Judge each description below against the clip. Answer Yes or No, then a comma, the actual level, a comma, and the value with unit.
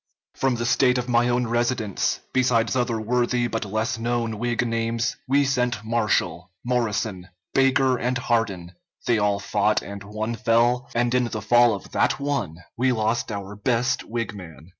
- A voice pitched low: Yes, low, 115 Hz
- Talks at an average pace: Yes, average, 165 wpm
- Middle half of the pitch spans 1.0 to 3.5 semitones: Yes, narrow, 2.4 semitones